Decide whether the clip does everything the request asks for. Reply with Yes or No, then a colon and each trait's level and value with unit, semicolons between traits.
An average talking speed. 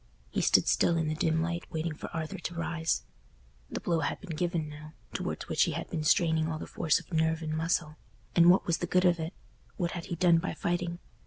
No: fast, 230 wpm